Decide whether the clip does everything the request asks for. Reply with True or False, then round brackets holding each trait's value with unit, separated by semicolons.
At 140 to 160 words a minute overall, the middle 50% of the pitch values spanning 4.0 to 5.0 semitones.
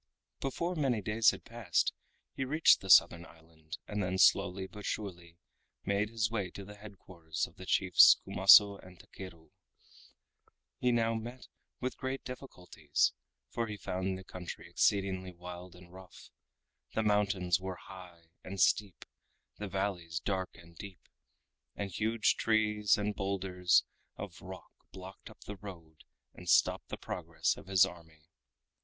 False (150 wpm; 3.0 semitones)